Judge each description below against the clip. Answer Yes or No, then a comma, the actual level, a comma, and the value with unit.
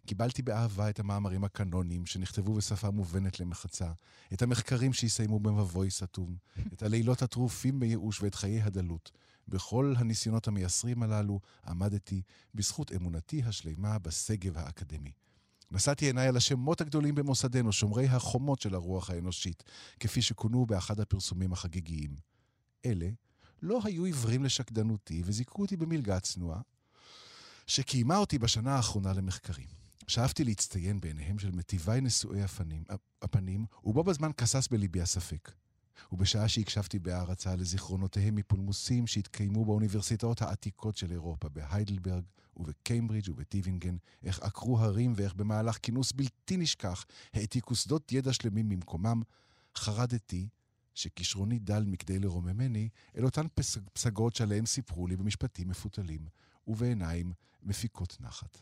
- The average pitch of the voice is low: Yes, low, 105 Hz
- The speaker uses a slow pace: No, average, 120 wpm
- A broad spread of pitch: No, average, 4.2 semitones